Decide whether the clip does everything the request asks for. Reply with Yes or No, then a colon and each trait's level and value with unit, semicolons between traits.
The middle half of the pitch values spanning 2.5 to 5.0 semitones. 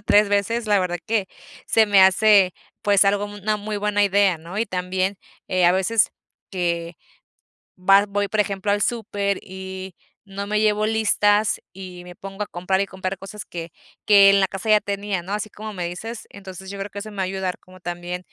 No: narrow, 1.8 semitones